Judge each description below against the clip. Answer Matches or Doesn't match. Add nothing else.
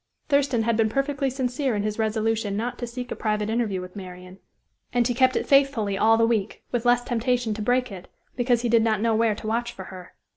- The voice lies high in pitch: Matches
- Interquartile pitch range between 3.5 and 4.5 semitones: Doesn't match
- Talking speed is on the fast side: Matches